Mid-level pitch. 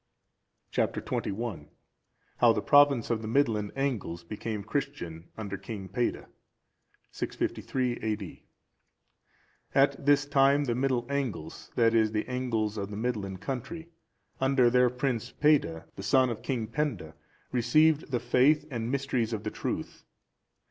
No: low, 120 Hz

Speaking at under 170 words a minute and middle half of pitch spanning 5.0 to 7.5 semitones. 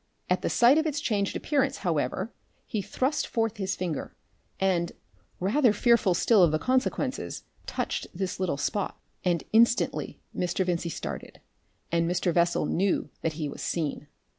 Yes: average, 155 wpm; wide, 5.5 semitones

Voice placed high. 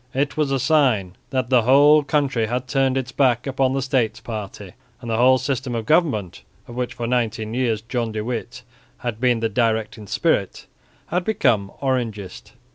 No: low, 125 Hz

